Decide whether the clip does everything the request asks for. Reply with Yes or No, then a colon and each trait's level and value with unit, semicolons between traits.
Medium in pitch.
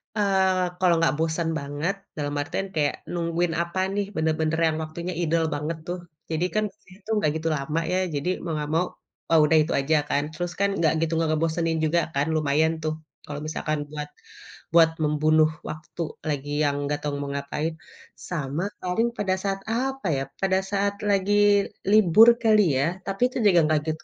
Yes: medium, 165 Hz